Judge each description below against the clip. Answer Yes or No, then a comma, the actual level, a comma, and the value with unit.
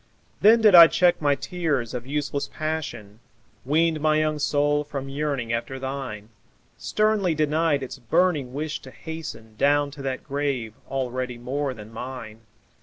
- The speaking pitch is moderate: Yes, medium, 145 Hz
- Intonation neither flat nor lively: Yes, average, 3.4 semitones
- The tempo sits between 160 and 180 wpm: No, average, 150 wpm